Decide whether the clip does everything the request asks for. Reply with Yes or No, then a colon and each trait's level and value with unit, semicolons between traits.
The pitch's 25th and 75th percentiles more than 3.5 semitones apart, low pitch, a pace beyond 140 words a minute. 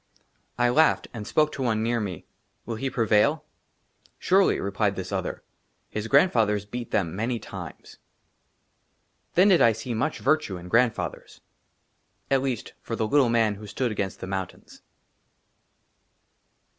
Yes: average, 4.1 semitones; low, 115 Hz; average, 160 wpm